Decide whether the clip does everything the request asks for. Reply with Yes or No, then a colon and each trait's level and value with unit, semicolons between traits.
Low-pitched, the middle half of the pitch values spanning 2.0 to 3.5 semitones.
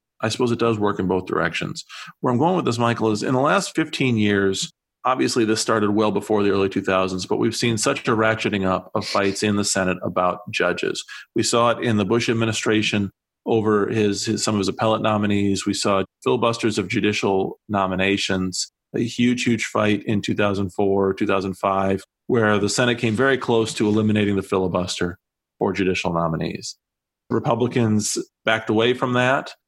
Yes: low, 105 Hz; average, 2.9 semitones